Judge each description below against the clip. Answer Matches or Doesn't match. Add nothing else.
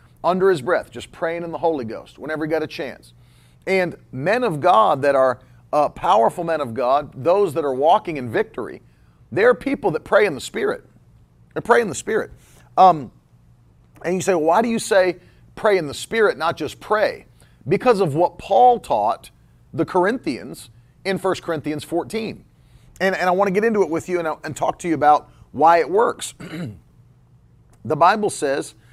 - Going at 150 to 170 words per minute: Doesn't match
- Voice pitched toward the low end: Doesn't match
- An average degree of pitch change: Doesn't match